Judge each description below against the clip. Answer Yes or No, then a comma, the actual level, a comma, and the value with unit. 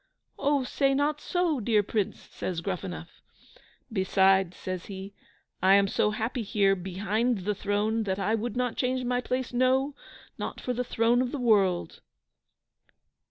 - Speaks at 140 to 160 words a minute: Yes, average, 155 wpm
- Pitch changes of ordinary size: Yes, average, 4.4 semitones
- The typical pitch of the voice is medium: No, high, 220 Hz